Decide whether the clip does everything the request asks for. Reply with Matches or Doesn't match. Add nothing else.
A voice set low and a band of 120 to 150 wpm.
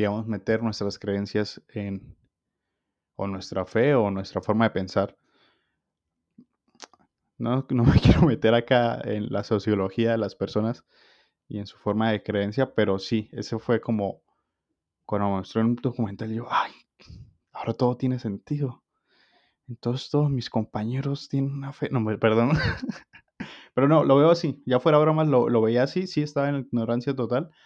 Doesn't match